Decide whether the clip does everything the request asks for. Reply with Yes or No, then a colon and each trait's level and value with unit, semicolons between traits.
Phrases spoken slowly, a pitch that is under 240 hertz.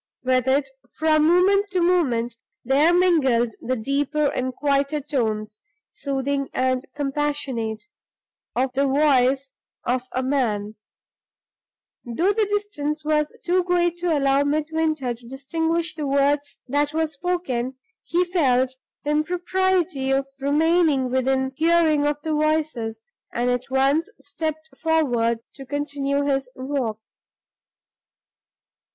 No: slow, 120 wpm; very high, 285 Hz